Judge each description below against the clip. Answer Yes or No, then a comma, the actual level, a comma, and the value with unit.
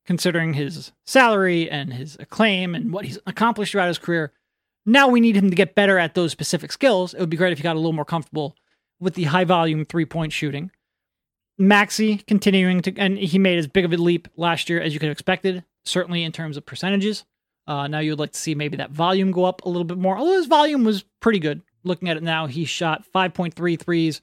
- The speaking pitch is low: No, medium, 175 Hz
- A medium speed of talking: No, fast, 235 wpm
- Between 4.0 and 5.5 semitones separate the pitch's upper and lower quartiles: No, average, 3.1 semitones